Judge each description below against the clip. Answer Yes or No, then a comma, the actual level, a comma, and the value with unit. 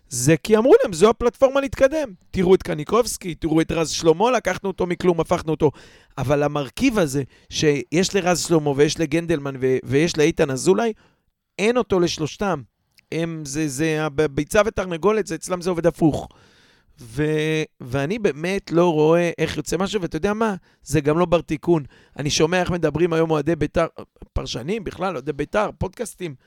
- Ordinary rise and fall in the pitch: Yes, average, 3.6 semitones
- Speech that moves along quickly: Yes, fast, 160 wpm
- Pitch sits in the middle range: Yes, medium, 165 Hz